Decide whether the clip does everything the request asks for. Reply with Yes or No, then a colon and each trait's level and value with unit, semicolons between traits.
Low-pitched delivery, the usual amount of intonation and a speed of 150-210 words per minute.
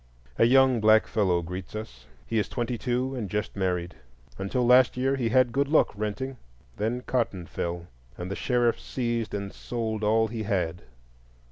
Yes: low, 110 Hz; average, 4.1 semitones; average, 170 wpm